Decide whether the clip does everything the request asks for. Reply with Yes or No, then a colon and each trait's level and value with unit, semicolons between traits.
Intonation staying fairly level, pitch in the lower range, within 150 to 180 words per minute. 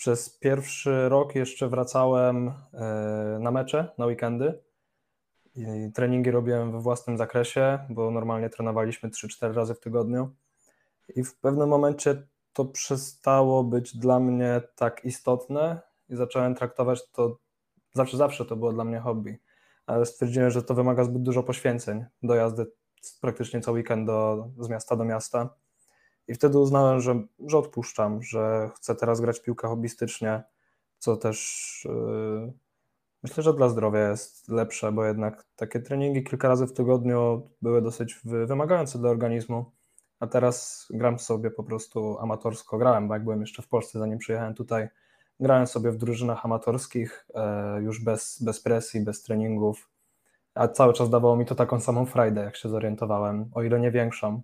Yes: narrow, 1.9 semitones; low, 120 Hz; average, 155 wpm